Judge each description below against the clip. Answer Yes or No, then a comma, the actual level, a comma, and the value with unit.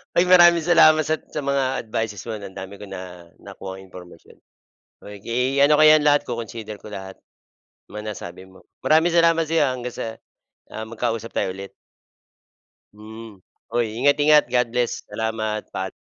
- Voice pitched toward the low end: Yes, low, 115 Hz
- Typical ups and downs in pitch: No, wide, 6.4 semitones